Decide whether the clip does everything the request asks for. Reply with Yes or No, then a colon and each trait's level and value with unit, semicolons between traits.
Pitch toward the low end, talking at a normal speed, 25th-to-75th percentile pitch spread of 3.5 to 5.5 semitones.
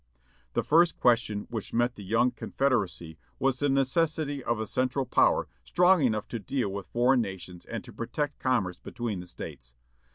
Yes: low, 120 Hz; average, 170 wpm; average, 4.8 semitones